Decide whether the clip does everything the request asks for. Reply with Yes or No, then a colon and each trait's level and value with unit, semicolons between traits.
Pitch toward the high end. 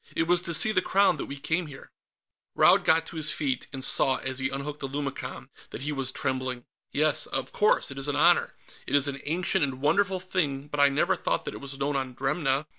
No: medium, 140 Hz